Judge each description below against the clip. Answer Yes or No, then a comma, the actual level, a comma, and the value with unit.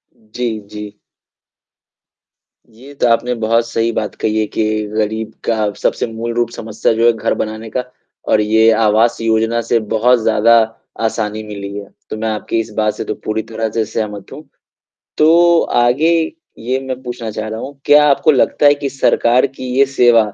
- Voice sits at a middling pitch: No, low, 115 Hz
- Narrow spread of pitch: Yes, narrow, 2.1 semitones